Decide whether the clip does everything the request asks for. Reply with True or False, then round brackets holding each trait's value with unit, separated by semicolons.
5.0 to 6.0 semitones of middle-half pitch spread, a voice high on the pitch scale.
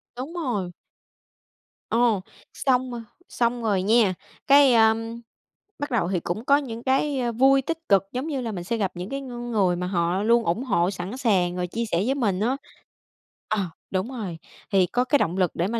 True (5.3 semitones; 230 Hz)